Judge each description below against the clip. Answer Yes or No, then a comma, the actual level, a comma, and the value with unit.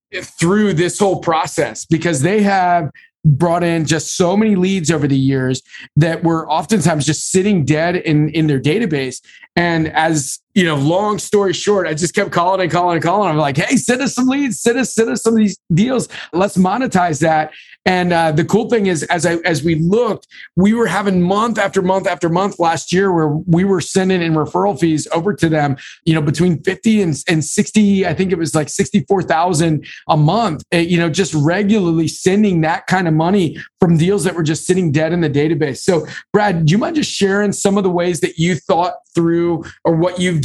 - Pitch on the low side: No, medium, 175 Hz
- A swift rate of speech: Yes, fast, 210 wpm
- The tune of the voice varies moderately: Yes, average, 3.5 semitones